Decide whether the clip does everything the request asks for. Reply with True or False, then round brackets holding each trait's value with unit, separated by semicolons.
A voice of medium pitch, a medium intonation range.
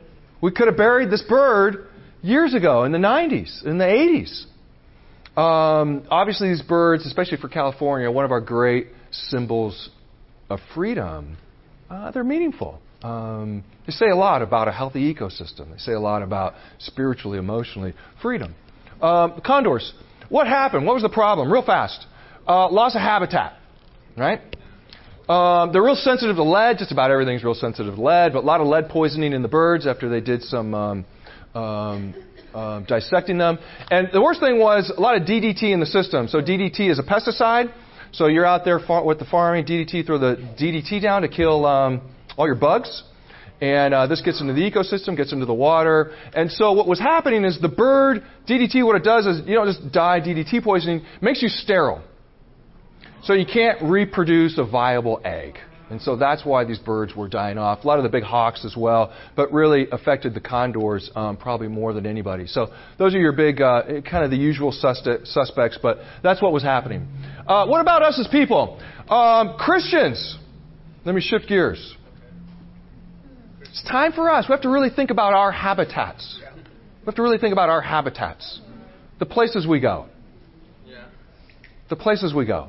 False (160 Hz; 8.5 semitones)